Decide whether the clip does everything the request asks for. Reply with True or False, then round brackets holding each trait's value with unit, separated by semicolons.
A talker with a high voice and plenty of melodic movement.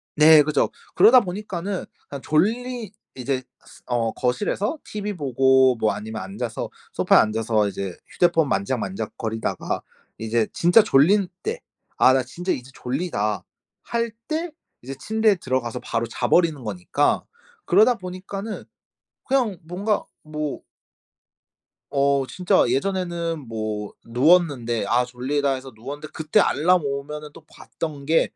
False (145 Hz; 7.2 semitones)